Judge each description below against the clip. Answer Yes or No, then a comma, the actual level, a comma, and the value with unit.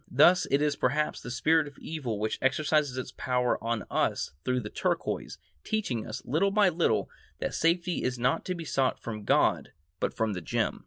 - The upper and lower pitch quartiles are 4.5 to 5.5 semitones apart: Yes, average, 5.0 semitones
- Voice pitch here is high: No, low, 135 Hz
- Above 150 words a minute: Yes, average, 195 wpm